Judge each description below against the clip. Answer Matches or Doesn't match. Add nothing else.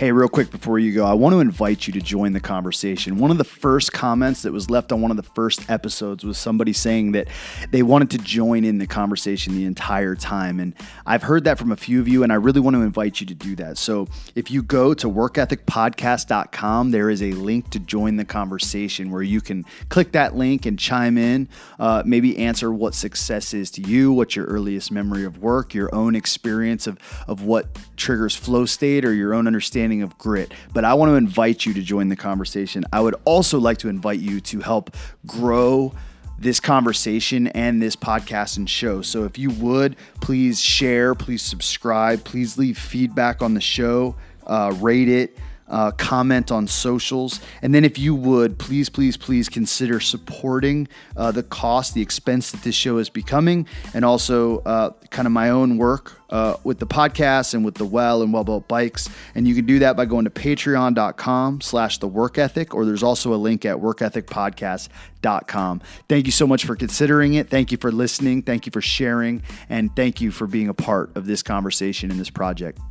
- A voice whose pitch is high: Doesn't match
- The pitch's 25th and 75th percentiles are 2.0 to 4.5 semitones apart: Matches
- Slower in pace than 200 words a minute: Doesn't match